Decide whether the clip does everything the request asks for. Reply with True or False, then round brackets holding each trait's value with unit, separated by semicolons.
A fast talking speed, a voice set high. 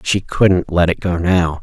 False (220 wpm; 90 Hz)